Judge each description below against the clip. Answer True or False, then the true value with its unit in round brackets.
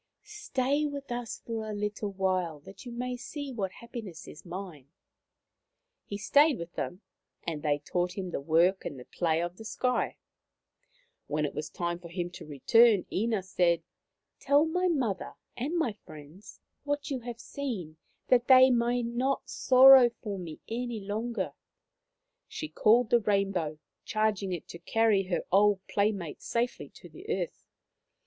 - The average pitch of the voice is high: True (210 Hz)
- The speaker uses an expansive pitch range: True (5.8 semitones)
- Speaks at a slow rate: False (165 wpm)